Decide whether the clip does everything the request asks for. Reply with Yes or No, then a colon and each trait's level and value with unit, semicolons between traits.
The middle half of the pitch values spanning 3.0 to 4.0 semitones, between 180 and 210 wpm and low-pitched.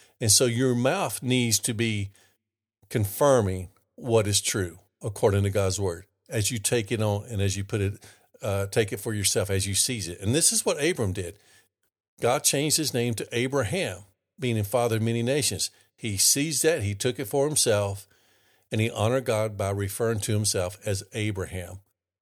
Yes: average, 3.5 semitones; average, 190 wpm; low, 110 Hz